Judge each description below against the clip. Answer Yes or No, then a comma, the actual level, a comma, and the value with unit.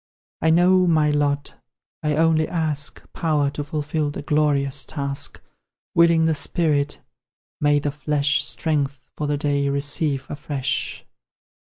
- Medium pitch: Yes, medium, 150 Hz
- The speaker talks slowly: Yes, slow, 130 wpm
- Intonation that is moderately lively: No, narrow, 1.8 semitones